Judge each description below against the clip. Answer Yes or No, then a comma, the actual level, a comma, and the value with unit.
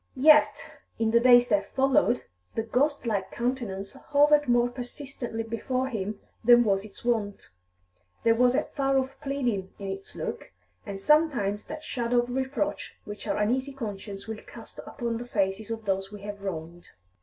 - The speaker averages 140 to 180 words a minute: Yes, average, 165 wpm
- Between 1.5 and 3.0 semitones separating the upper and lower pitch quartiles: No, average, 4.3 semitones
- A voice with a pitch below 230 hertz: No, high, 235 Hz